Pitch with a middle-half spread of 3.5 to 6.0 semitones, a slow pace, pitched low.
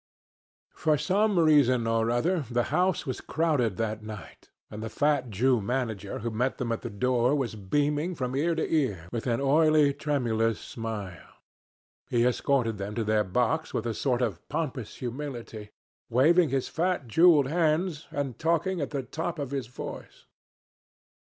No: average, 5.1 semitones; average, 165 wpm; low, 130 Hz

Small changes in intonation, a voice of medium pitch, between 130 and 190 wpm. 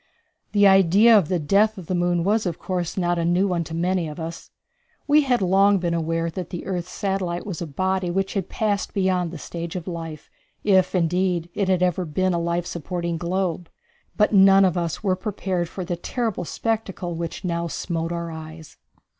No: narrow, 2.3 semitones; medium, 180 Hz; average, 200 wpm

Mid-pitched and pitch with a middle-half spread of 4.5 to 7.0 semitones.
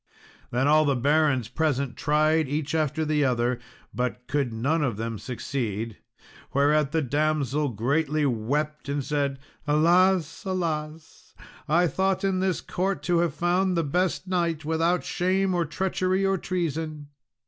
No: medium, 155 Hz; average, 3.8 semitones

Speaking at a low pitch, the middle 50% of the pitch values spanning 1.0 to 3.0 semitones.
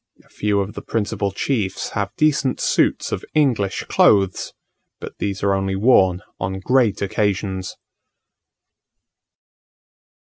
Yes: low, 100 Hz; narrow, 2.6 semitones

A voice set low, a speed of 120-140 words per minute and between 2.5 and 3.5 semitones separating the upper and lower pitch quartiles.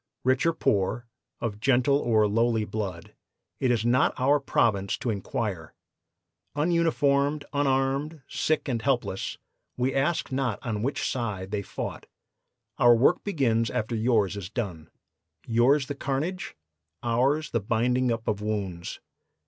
No: low, 120 Hz; slow, 135 wpm; average, 4.3 semitones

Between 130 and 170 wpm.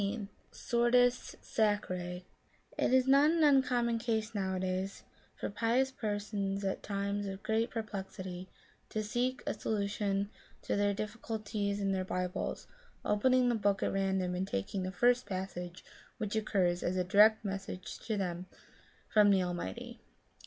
Yes: average, 145 wpm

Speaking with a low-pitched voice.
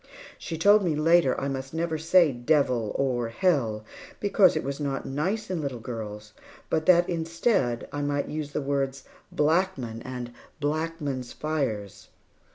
No: medium, 145 Hz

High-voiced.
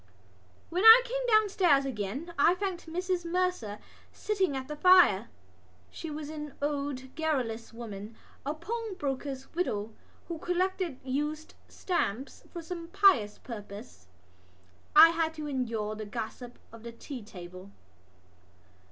Yes: very high, 295 Hz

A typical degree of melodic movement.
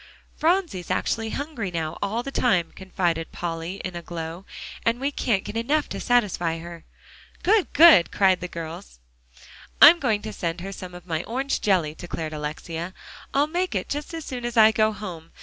No: wide, 6.5 semitones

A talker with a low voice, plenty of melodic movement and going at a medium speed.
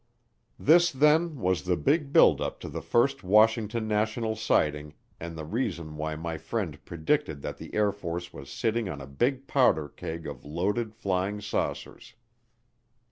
Yes: low, 100 Hz; wide, 6.5 semitones; average, 160 wpm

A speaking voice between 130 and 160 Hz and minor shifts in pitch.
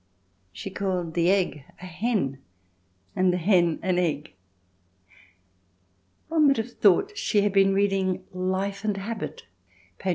No: high, 190 Hz; narrow, 2.2 semitones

